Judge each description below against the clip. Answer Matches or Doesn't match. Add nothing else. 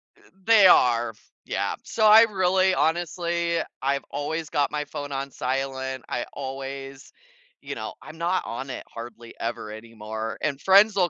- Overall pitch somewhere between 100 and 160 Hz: Matches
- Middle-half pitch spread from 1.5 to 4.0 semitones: Doesn't match